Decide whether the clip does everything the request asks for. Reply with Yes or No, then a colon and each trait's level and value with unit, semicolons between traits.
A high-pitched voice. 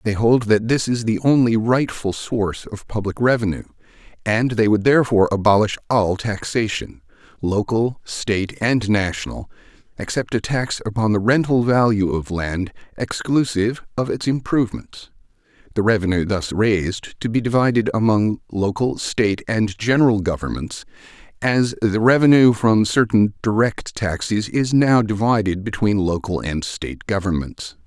No: low, 110 Hz